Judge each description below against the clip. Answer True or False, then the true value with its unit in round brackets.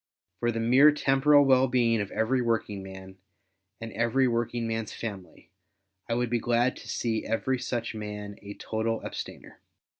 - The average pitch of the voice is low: True (115 Hz)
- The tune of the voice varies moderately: False (2.1 semitones)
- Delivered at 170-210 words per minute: False (160 wpm)